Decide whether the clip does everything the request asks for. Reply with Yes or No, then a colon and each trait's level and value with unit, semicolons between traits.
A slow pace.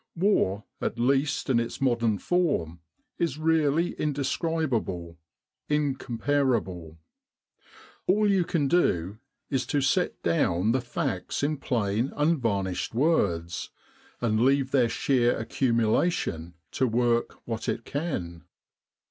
Yes: slow, 115 wpm